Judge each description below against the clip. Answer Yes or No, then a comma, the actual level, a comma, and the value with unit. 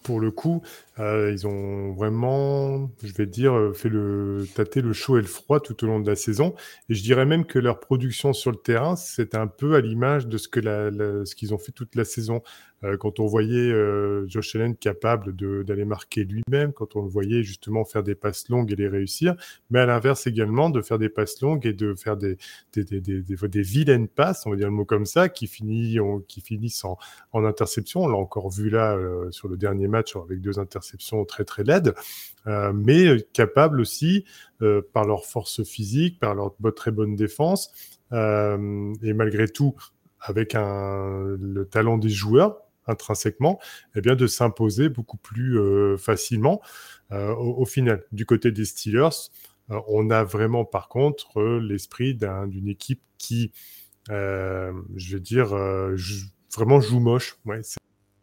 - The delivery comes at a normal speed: Yes, average, 195 wpm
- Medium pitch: No, low, 110 Hz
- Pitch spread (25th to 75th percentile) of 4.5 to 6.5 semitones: No, average, 3.1 semitones